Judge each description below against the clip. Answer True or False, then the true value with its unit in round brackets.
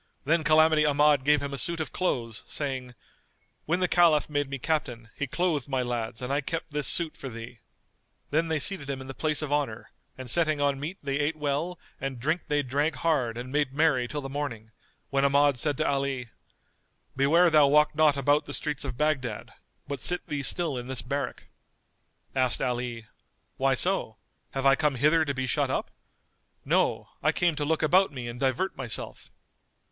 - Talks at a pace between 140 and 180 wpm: False (195 wpm)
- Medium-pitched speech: True (145 Hz)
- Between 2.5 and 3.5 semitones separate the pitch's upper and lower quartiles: True (2.9 semitones)